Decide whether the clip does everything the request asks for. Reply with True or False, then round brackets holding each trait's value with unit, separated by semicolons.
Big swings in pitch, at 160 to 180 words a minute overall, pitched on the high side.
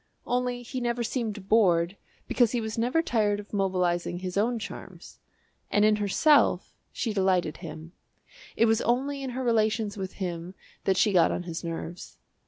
False (4.4 semitones; 170 wpm; 210 Hz)